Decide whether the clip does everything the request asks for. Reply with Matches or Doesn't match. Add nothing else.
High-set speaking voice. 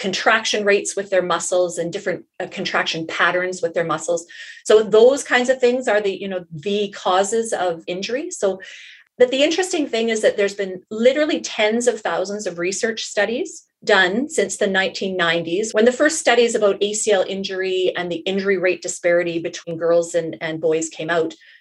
Matches